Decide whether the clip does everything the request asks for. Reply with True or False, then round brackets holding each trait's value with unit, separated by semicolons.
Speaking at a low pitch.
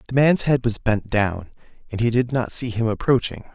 True (115 Hz)